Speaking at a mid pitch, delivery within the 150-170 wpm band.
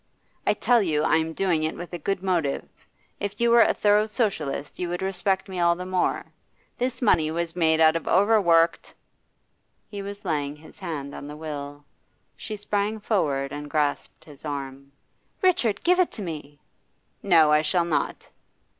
No: medium, 170 Hz; average, 180 wpm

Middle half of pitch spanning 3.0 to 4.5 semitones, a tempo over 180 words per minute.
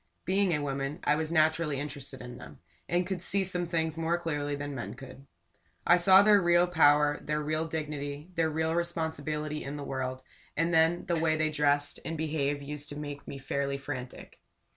No: narrow, 2.6 semitones; average, 190 wpm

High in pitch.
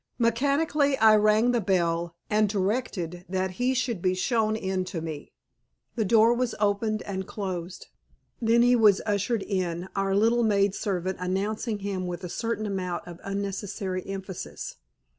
Yes: high, 200 Hz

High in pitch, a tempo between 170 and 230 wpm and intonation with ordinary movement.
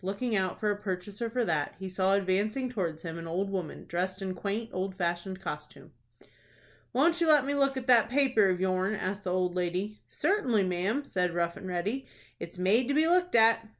Yes: high, 195 Hz; fast, 205 wpm; average, 4.8 semitones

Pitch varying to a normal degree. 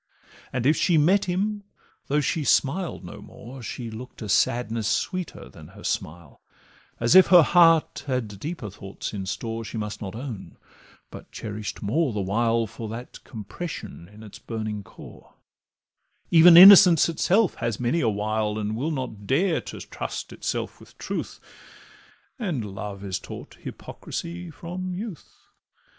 No: wide, 7.9 semitones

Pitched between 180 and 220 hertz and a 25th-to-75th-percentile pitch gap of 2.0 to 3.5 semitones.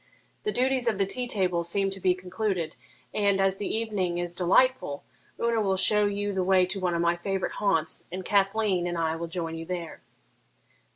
Yes: high, 190 Hz; average, 2.9 semitones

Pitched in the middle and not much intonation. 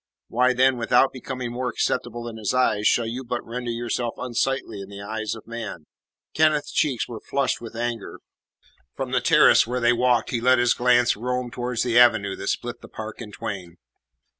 No: low, 120 Hz; narrow, 1.9 semitones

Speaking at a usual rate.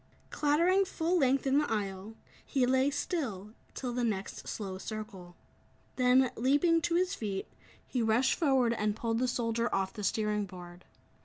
Yes: average, 160 wpm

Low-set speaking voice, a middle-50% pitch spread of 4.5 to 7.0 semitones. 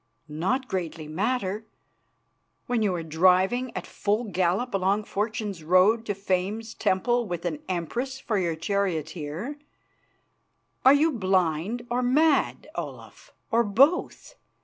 No: high, 200 Hz; average, 5.1 semitones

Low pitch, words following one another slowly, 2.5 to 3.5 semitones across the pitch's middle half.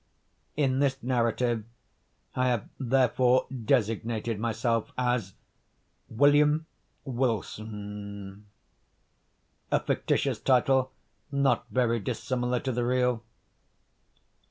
Yes: low, 125 Hz; slow, 80 wpm; average, 2.8 semitones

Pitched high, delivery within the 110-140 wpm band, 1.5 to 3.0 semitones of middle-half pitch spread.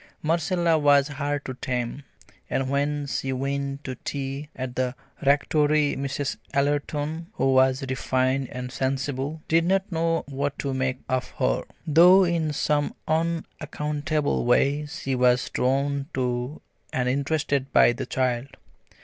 No: medium, 140 Hz; slow, 135 wpm; narrow, 2.4 semitones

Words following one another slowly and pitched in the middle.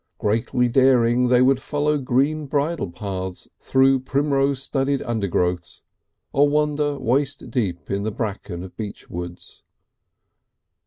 No: slow, 120 wpm; low, 125 Hz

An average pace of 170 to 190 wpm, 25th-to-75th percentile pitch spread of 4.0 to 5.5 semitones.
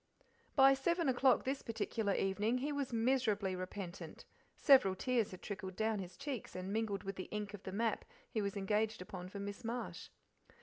Yes: average, 180 wpm; average, 4.4 semitones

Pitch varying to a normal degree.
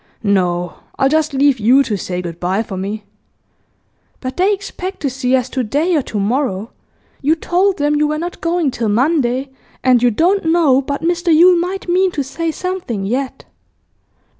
No: wide, 6.7 semitones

